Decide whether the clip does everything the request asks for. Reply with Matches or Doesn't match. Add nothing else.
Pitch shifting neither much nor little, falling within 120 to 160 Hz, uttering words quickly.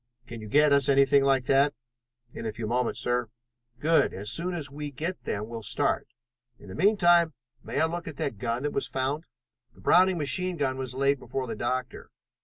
Matches